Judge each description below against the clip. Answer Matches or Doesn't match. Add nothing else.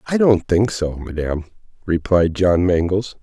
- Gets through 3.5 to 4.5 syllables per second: Matches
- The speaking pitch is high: Doesn't match